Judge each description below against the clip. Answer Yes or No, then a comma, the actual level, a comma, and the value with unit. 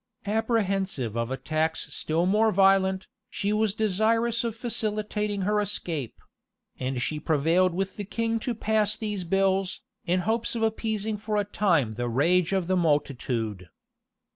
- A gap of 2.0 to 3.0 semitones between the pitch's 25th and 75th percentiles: No, average, 5.0 semitones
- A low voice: No, high, 195 Hz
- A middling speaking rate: Yes, average, 150 wpm